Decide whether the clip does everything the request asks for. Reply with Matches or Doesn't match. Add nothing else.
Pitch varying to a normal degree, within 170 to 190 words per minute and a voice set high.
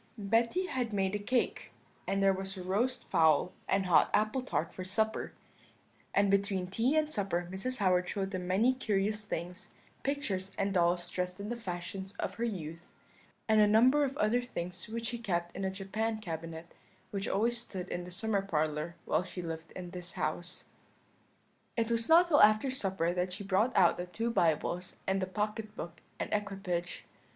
Matches